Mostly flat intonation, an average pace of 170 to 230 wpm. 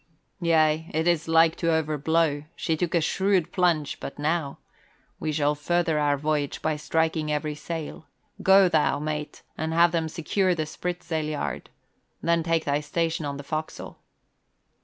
No: narrow, 1.9 semitones; average, 160 wpm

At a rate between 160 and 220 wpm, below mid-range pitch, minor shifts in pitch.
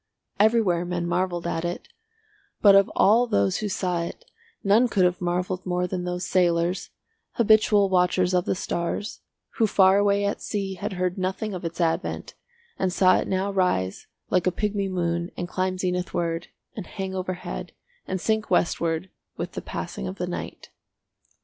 No: average, 170 wpm; medium, 185 Hz; narrow, 2.1 semitones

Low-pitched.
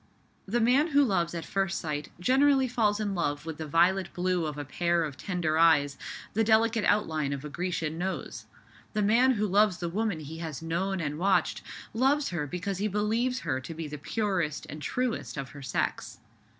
No: medium, 180 Hz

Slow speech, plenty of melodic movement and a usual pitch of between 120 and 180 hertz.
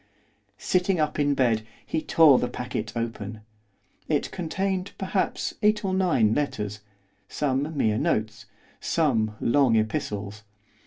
Yes: slow, 120 wpm; wide, 7.1 semitones; low, 135 Hz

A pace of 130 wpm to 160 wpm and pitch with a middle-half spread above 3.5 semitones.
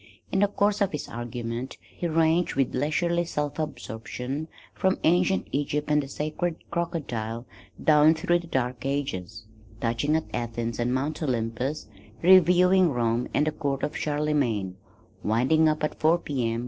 Yes: average, 155 wpm; average, 5.2 semitones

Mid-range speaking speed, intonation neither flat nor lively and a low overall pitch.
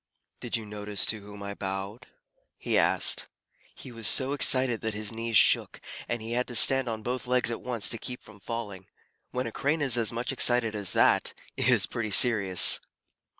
Yes: average, 195 wpm; average, 3.0 semitones; low, 115 Hz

